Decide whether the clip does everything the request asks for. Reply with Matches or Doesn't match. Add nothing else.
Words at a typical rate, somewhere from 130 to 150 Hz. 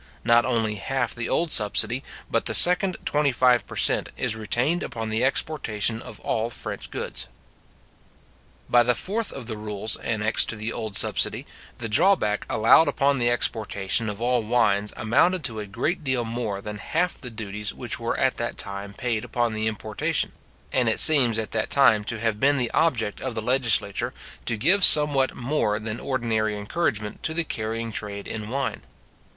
Doesn't match